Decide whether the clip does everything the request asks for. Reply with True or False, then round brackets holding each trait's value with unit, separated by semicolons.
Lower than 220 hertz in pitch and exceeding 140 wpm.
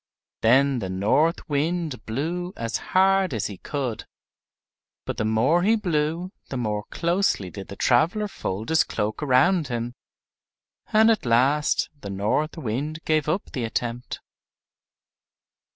False (140 Hz; 135 wpm)